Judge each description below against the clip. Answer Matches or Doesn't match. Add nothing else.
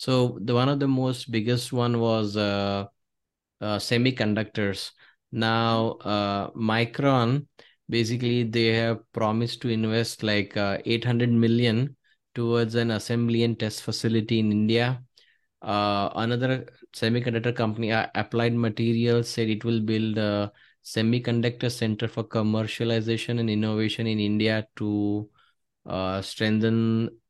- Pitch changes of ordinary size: Doesn't match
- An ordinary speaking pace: Doesn't match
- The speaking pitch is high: Doesn't match